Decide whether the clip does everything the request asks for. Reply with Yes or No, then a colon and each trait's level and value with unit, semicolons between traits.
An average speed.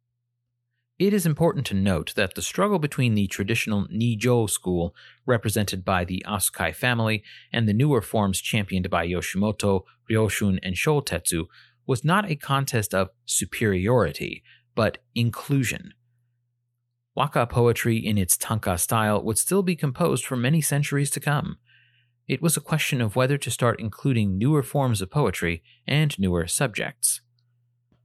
Yes: average, 145 wpm